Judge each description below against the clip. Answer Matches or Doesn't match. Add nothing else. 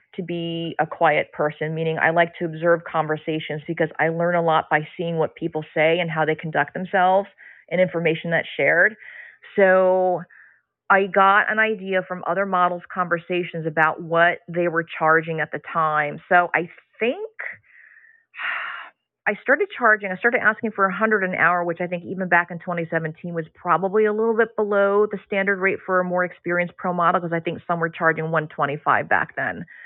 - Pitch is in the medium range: Matches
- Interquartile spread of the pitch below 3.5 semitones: Matches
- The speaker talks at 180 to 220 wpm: Matches